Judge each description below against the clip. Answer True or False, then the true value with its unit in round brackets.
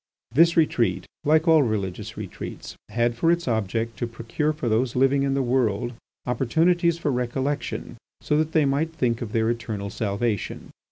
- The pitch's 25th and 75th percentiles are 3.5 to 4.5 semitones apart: False (4.9 semitones)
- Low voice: True (125 Hz)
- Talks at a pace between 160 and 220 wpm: True (165 wpm)